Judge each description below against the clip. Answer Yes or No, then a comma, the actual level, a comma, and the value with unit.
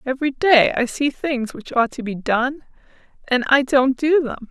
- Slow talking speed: No, average, 200 wpm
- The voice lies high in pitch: Yes, very high, 265 Hz